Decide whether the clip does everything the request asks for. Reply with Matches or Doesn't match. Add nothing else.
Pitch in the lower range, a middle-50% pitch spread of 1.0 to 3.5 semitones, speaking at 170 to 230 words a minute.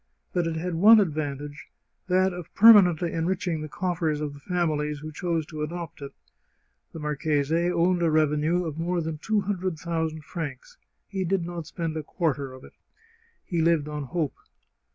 Doesn't match